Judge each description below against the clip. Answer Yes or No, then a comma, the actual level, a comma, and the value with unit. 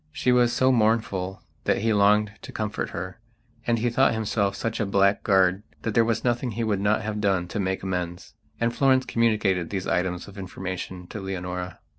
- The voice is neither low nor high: No, low, 100 Hz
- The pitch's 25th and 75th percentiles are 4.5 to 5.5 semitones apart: No, average, 3.4 semitones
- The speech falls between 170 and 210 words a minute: Yes, average, 190 wpm